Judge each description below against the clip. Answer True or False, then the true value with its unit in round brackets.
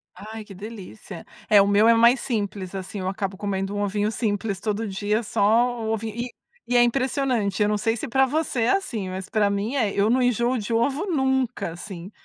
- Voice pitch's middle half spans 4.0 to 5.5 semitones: False (3.1 semitones)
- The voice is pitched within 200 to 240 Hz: True (215 Hz)